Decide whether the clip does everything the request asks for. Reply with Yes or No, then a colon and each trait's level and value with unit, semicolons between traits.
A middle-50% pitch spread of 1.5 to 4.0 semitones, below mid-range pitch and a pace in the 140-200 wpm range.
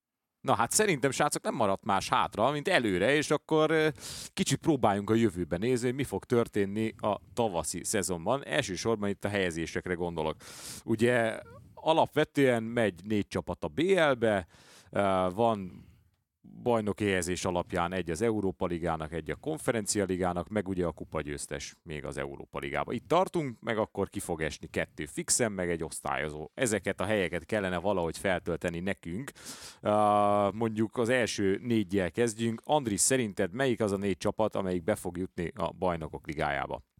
No: average, 4.5 semitones; low, 100 Hz; fast, 155 wpm